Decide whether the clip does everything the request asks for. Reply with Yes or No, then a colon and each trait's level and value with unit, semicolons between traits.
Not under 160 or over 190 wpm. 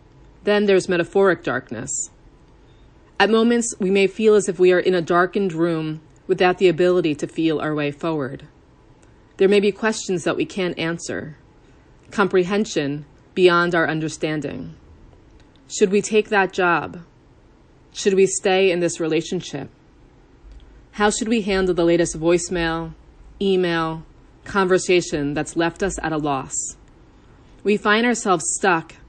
No: average, 140 wpm